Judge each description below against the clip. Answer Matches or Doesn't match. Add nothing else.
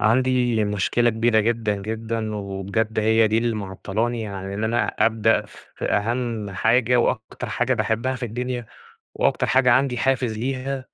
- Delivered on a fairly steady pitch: Matches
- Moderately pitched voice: Doesn't match